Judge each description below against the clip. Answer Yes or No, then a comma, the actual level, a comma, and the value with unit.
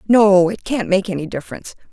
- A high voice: Yes, high, 195 Hz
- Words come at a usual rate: Yes, average, 190 wpm